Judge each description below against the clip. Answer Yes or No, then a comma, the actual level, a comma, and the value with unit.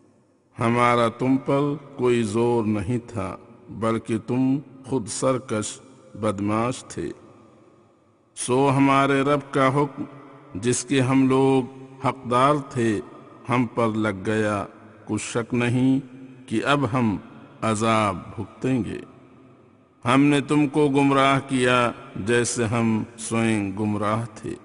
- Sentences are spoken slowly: Yes, slow, 115 wpm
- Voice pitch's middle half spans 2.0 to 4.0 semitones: Yes, average, 3.1 semitones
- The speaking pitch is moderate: No, low, 120 Hz